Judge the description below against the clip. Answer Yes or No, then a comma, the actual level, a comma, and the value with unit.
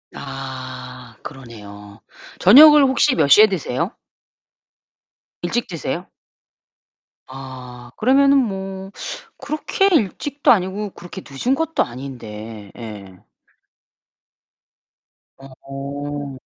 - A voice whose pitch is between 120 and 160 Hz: Yes, medium, 140 Hz